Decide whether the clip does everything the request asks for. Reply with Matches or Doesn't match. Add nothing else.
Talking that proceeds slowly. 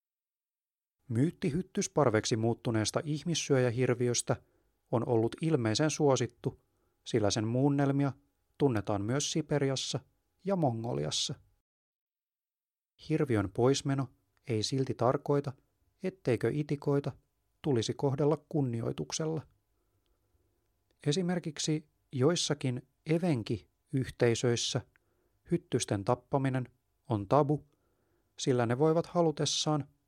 Matches